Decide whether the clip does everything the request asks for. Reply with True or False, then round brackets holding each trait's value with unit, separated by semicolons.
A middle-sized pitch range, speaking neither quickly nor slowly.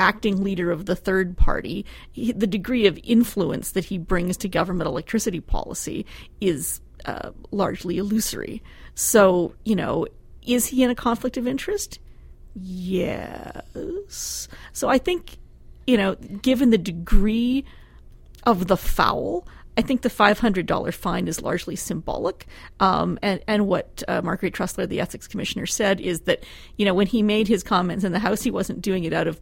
True (4.1 semitones; 165 wpm)